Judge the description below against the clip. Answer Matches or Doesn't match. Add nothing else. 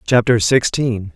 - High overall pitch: Doesn't match